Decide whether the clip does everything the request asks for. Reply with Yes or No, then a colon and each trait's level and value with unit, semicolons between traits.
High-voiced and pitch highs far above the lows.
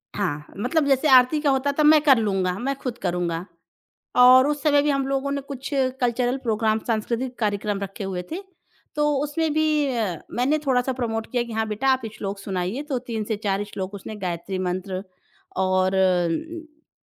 Yes: high, 240 Hz; wide, 5.9 semitones